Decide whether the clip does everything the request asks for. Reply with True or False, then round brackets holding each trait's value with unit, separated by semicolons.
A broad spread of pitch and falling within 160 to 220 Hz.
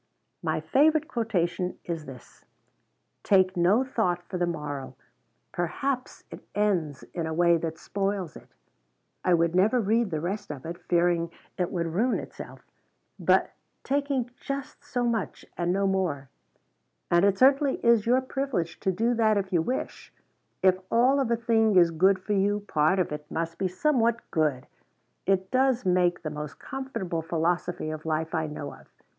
True (5.7 semitones; 185 Hz)